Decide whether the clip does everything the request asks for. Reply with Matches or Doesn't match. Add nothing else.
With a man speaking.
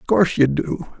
Matches